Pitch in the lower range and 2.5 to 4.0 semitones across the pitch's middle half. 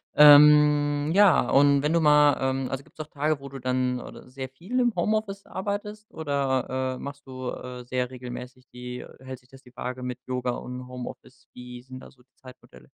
Yes: low, 130 Hz; average, 2.8 semitones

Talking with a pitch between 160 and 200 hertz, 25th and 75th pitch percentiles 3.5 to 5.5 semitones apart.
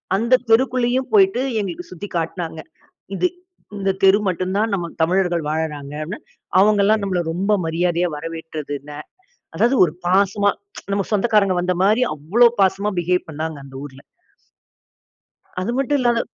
Yes: high, 190 Hz; average, 4.6 semitones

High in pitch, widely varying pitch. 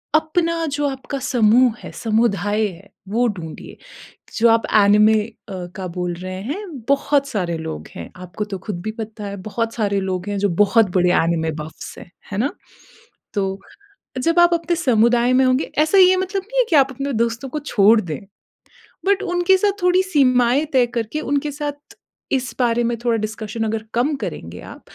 Yes: high, 235 Hz; wide, 6.2 semitones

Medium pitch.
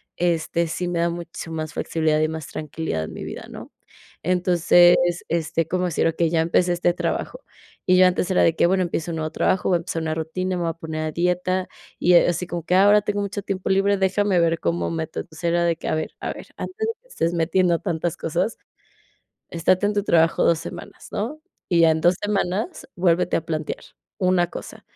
Yes: medium, 175 Hz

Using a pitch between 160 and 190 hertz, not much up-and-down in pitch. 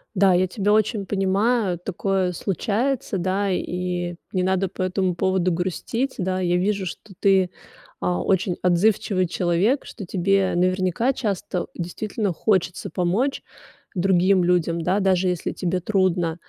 Yes: medium, 185 Hz; narrow, 2.0 semitones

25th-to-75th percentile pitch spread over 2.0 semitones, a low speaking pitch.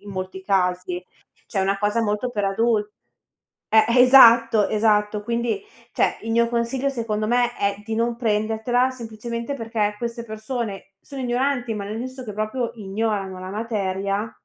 No: narrow, 2.4 semitones; high, 220 Hz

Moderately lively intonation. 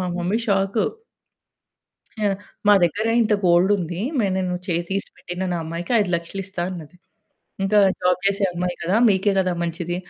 No: narrow, 2.2 semitones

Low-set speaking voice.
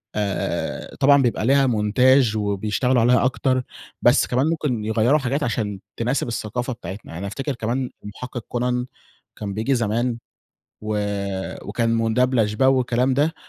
Yes: low, 120 Hz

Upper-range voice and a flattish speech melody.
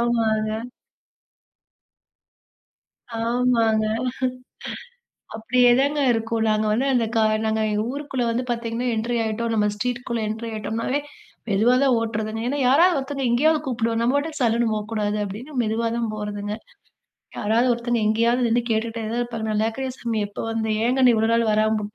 Yes: high, 230 Hz; narrow, 2.1 semitones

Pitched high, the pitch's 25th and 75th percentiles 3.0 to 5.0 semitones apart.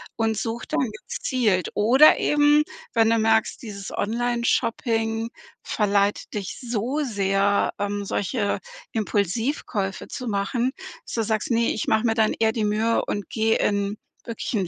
No: high, 220 Hz; narrow, 2.5 semitones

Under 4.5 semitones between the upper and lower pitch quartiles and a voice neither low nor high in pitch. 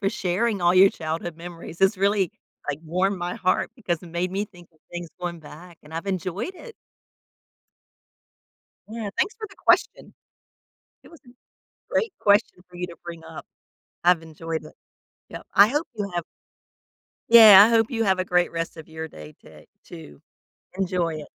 Yes: average, 3.5 semitones; medium, 180 Hz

